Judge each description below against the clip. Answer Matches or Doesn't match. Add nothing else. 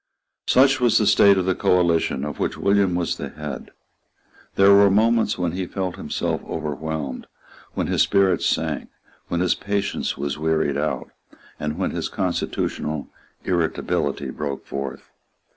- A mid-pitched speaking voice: Doesn't match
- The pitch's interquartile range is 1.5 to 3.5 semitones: Doesn't match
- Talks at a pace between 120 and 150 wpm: Matches